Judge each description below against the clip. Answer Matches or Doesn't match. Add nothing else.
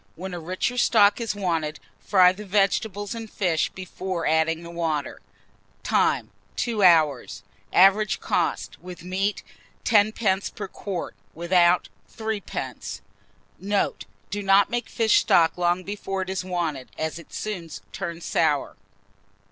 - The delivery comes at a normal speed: Doesn't match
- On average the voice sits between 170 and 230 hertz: Matches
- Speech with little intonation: Doesn't match